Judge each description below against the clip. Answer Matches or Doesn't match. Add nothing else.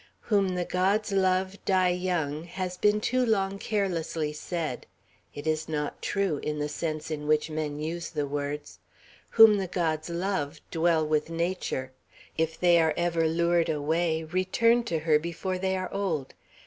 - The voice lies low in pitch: Doesn't match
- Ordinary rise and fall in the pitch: Matches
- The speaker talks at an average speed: Matches